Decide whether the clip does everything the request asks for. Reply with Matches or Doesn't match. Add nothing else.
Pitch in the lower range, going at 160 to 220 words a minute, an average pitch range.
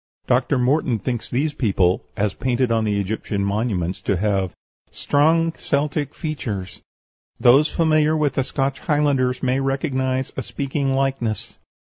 Doesn't match